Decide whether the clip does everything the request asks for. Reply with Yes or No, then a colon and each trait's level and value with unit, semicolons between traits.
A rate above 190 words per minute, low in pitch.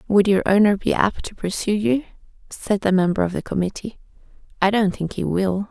No: average, 200 wpm; high, 200 Hz